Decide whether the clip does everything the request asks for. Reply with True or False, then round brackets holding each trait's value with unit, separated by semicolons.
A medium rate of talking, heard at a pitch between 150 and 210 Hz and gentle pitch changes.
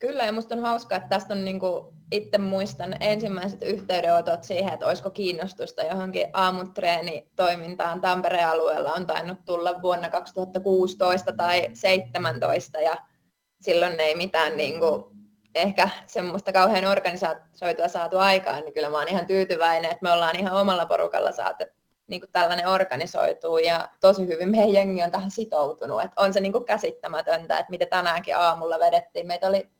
False (160 wpm; 185 Hz; 2.3 semitones)